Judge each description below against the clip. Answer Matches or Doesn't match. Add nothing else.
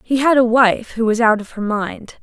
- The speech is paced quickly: Matches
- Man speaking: Doesn't match